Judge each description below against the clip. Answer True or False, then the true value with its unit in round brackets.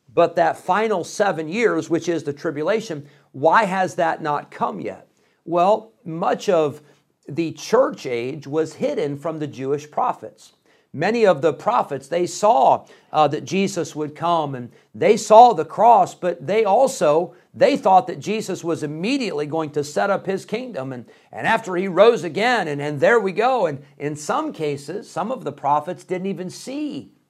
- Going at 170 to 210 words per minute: True (175 wpm)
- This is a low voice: False (165 Hz)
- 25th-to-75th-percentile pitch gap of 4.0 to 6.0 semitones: True (5.3 semitones)